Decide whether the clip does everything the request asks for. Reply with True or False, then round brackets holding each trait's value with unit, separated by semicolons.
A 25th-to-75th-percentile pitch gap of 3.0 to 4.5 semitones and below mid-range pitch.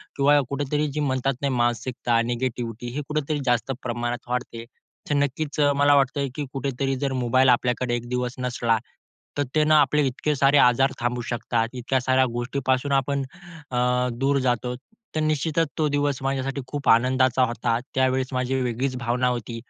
False (2.4 semitones; 130 Hz)